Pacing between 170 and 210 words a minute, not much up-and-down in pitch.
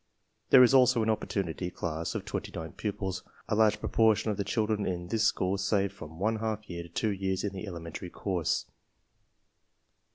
No: average, 185 wpm; average, 3.4 semitones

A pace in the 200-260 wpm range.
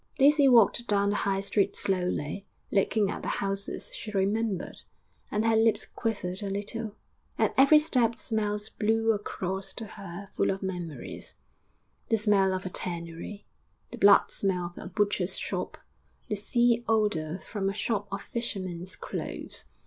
No: average, 155 wpm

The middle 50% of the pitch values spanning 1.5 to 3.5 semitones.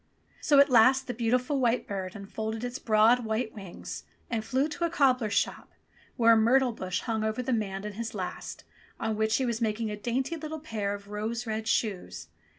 Yes: average, 2.9 semitones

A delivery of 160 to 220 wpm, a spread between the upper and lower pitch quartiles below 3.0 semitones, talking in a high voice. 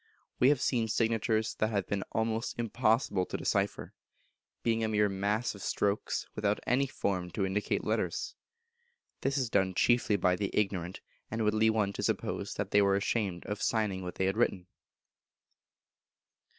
No: average, 165 wpm; narrow, 2.4 semitones; low, 105 Hz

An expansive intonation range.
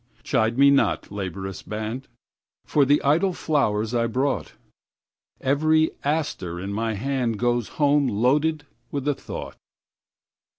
No: average, 4.9 semitones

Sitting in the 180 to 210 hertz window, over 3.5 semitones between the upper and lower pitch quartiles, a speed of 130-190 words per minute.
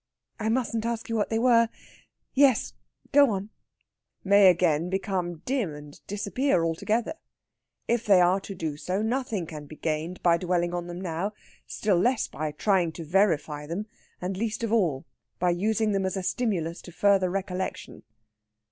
Yes: high, 190 Hz; average, 4.3 semitones; average, 165 wpm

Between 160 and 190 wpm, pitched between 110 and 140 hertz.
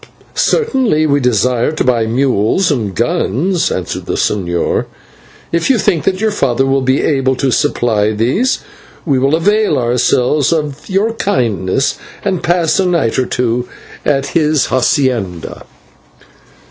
No: average, 145 wpm; low, 135 Hz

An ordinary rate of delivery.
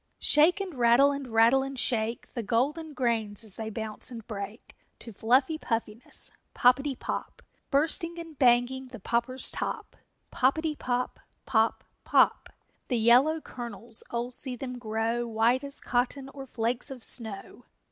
Yes: average, 150 wpm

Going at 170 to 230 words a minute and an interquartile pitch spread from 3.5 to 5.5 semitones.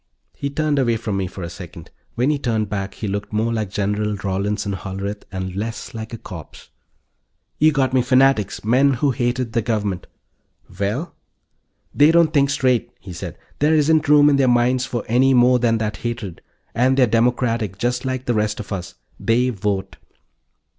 Yes: average, 180 wpm; average, 4.1 semitones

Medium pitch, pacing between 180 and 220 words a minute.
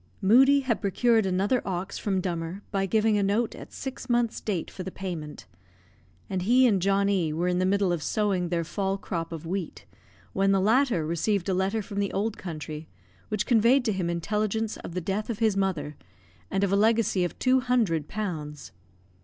No: high, 195 Hz; average, 195 wpm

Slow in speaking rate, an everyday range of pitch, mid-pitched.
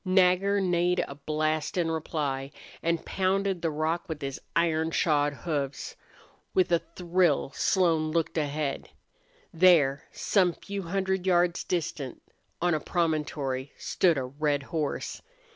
Yes: slow, 130 wpm; average, 3.3 semitones; medium, 165 Hz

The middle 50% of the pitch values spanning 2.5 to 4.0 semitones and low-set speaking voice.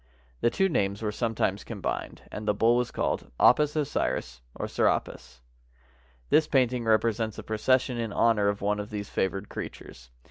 Yes: average, 3.2 semitones; low, 110 Hz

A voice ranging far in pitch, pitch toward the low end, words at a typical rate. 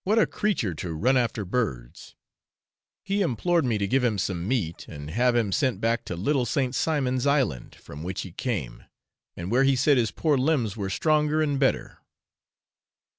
Yes: wide, 6.6 semitones; low, 125 Hz; average, 180 wpm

